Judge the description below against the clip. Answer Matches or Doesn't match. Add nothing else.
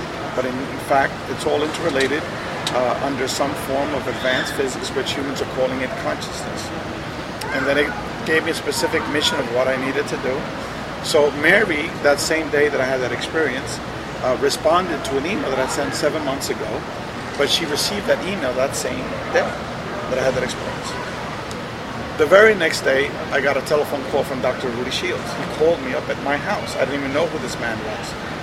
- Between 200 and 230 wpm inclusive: Matches